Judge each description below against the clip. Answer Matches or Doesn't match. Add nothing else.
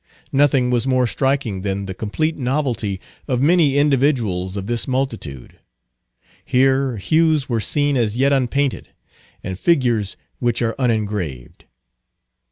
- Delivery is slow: Matches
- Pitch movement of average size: Matches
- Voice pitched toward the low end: Matches